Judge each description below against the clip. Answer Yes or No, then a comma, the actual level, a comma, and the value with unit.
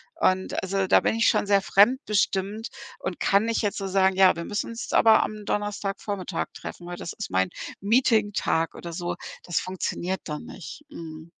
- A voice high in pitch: Yes, high, 195 Hz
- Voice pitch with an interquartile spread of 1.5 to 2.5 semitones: No, average, 2.9 semitones